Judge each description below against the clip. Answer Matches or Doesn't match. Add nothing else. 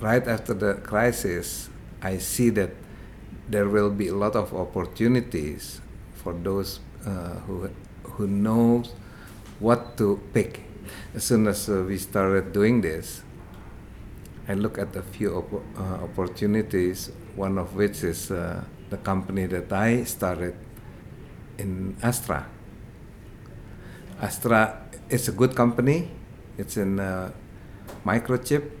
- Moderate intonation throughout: Matches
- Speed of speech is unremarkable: Doesn't match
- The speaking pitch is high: Doesn't match